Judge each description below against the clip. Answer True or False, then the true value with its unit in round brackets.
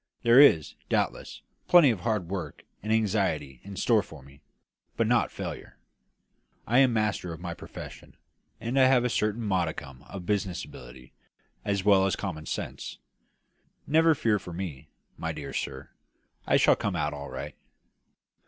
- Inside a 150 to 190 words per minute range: True (160 wpm)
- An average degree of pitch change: False (6.5 semitones)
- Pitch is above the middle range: False (95 Hz)